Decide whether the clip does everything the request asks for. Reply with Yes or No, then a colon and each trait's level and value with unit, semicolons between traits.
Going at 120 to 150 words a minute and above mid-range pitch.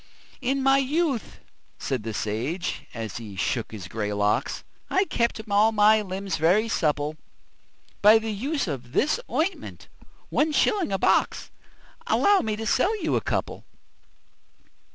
Yes: average, 145 wpm; high, 210 Hz